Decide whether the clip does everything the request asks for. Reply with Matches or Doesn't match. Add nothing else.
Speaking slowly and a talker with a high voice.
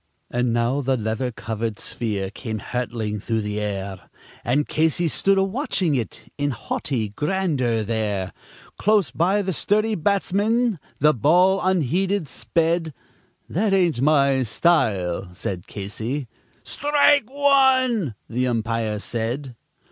Doesn't match